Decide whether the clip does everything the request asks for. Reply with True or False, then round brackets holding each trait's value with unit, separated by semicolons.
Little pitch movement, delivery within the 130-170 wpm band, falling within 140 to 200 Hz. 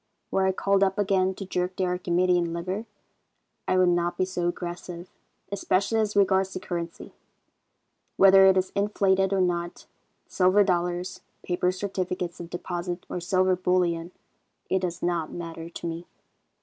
True (1.6 semitones; 150 wpm; 185 Hz)